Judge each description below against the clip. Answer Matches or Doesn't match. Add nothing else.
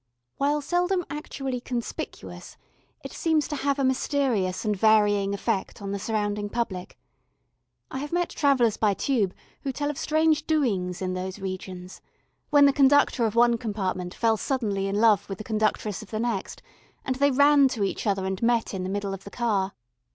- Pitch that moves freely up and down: Matches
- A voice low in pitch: Doesn't match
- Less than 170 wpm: Doesn't match